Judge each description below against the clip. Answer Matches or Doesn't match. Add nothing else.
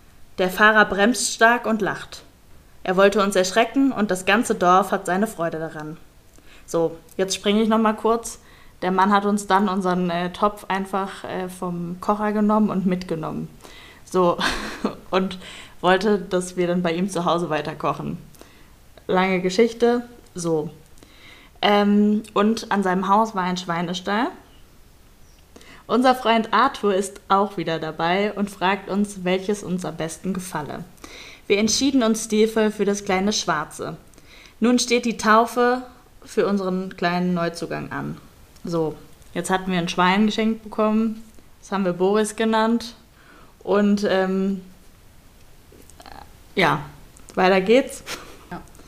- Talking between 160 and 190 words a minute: Doesn't match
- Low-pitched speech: Doesn't match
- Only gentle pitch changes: Doesn't match